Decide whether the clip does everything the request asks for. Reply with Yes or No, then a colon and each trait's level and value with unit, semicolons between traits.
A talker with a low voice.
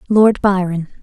No: high, 190 Hz